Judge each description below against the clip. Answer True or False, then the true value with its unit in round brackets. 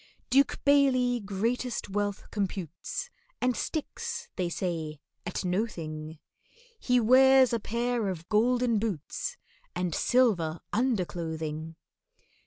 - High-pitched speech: True (210 Hz)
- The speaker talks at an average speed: False (105 wpm)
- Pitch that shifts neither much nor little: False (6.3 semitones)